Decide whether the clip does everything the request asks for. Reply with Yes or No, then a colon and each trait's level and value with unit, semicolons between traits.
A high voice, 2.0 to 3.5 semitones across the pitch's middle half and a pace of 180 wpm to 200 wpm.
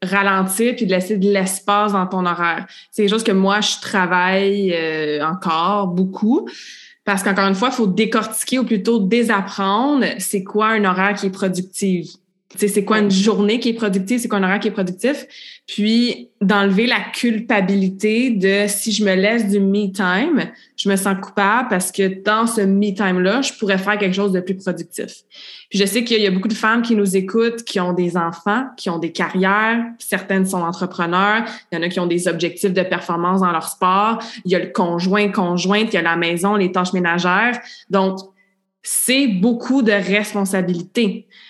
Yes: high, 200 Hz; average, 2.7 semitones; average, 195 wpm